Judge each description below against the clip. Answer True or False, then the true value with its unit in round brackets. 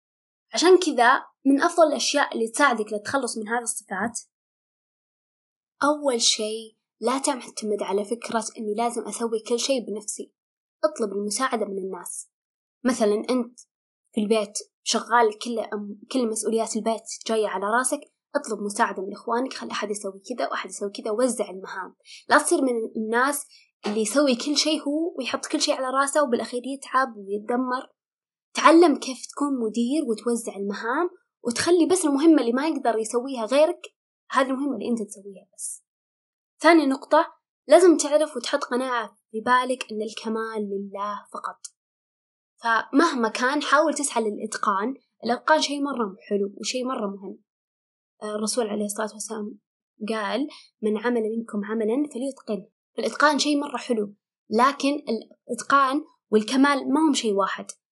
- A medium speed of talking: False (140 wpm)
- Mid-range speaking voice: False (240 Hz)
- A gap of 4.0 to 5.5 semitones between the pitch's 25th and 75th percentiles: True (4.6 semitones)